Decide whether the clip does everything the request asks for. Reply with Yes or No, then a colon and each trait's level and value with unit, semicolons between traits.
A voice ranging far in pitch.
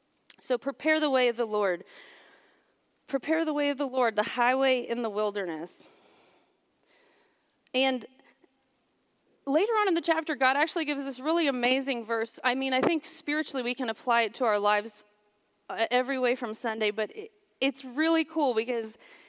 No: average, 5.0 semitones